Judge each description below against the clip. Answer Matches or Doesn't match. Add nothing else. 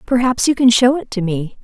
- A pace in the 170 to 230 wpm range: Doesn't match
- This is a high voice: Matches